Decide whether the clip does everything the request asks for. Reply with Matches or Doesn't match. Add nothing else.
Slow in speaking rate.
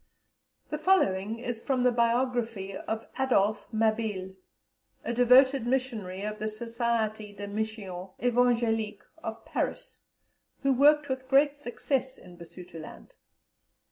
Matches